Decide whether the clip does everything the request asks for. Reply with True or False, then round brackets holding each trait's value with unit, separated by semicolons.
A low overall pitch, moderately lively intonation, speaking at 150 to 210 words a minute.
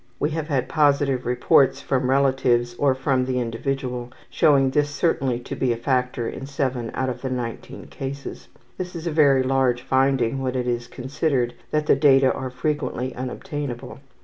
False (130 Hz; 2.1 semitones; 175 wpm)